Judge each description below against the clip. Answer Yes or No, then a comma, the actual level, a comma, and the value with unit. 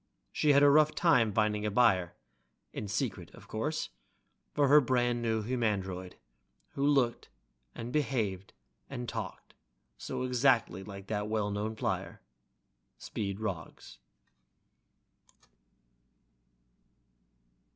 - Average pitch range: Yes, average, 4.0 semitones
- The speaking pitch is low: Yes, low, 110 Hz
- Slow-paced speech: Yes, slow, 110 wpm